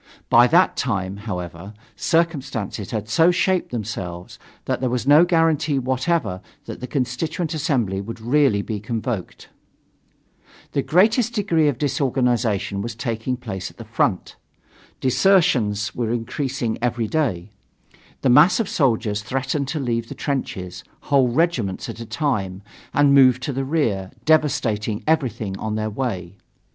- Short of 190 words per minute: Yes, average, 140 wpm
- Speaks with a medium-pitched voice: No, low, 125 Hz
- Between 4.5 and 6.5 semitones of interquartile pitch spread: Yes, wide, 5.5 semitones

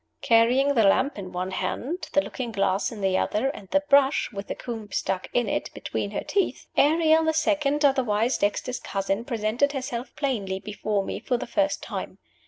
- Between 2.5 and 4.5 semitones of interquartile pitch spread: No, wide, 5.6 semitones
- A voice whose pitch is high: Yes, high, 240 Hz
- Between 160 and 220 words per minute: Yes, average, 190 wpm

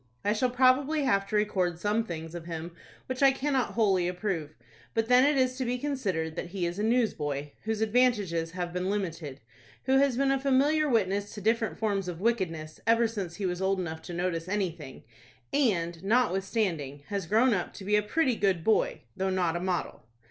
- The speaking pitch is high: Yes, high, 200 Hz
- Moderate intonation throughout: No, wide, 5.7 semitones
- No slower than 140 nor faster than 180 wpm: No, average, 200 wpm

